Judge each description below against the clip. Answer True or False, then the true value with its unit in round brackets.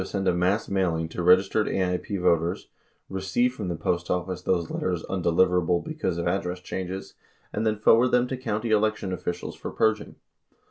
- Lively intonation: False (3.3 semitones)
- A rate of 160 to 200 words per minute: True (175 wpm)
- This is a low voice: True (95 Hz)